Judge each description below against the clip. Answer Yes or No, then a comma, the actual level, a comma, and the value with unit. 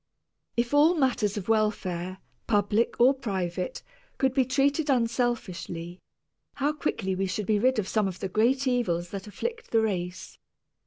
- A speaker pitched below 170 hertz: No, high, 220 Hz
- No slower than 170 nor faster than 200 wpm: No, average, 155 wpm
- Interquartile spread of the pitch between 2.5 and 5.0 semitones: No, wide, 5.6 semitones